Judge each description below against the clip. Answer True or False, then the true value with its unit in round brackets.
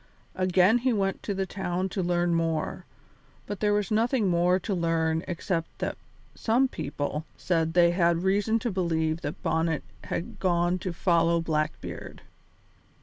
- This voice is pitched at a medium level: True (175 Hz)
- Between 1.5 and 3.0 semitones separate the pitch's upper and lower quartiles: True (2.7 semitones)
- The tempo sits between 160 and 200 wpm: False (150 wpm)